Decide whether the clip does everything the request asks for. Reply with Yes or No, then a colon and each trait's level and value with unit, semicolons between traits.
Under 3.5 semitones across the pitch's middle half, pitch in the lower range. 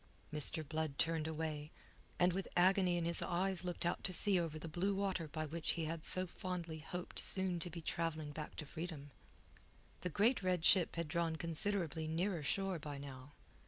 No: narrow, 2.6 semitones; medium, 170 Hz